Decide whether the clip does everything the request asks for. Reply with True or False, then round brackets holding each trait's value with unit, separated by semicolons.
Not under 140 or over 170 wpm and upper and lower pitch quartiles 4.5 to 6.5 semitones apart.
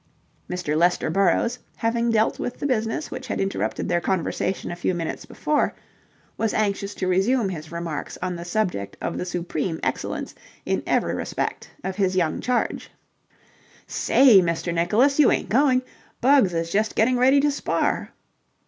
True (160 wpm; 5.5 semitones)